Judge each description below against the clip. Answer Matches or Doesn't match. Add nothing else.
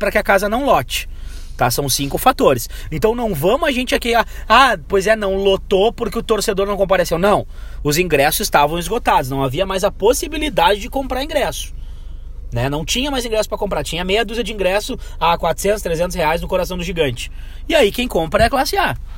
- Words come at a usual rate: Doesn't match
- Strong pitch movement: Matches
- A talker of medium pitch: Doesn't match